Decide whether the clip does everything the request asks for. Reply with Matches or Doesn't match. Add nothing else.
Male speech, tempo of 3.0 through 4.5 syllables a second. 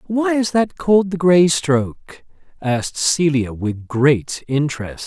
Matches